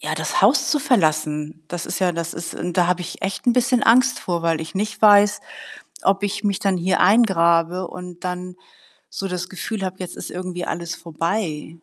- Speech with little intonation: No, average, 3.1 semitones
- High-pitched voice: No, medium, 180 Hz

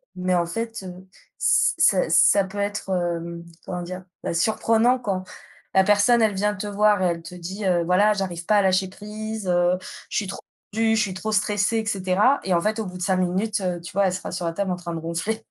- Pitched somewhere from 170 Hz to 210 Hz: Yes, high, 190 Hz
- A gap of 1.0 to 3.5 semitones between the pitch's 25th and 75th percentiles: Yes, average, 2.9 semitones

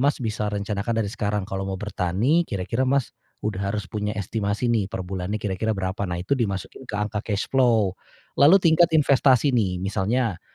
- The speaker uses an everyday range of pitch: Yes, average, 4.0 semitones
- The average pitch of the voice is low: Yes, low, 105 Hz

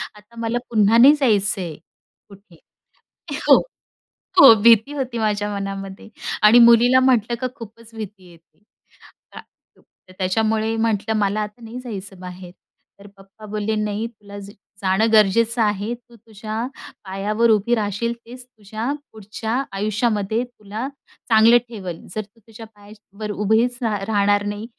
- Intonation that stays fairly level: Yes, narrow, 2.2 semitones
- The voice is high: Yes, high, 215 Hz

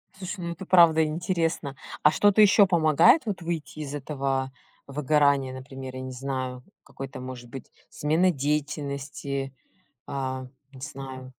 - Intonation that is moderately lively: Yes, average, 3.6 semitones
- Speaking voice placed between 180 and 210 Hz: No, medium, 140 Hz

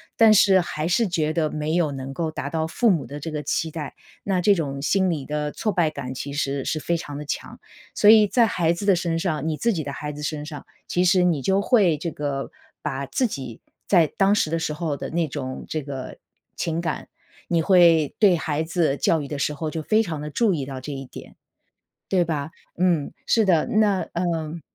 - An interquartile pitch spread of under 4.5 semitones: Yes, average, 3.5 semitones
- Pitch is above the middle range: No, medium, 160 Hz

